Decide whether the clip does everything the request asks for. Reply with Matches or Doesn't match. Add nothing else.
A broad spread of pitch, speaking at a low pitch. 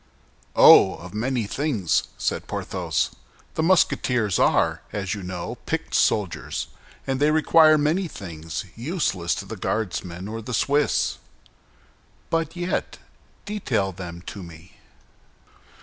Matches